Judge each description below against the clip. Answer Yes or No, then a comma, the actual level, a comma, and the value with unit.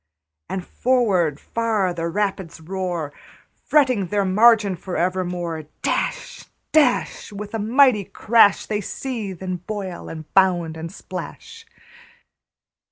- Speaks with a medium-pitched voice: No, high, 195 Hz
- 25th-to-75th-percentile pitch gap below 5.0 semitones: Yes, average, 4.2 semitones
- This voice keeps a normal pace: No, slow, 115 wpm